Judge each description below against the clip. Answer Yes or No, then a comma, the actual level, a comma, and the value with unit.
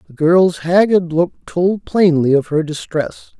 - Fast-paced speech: No, average, 160 wpm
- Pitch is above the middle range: No, medium, 165 Hz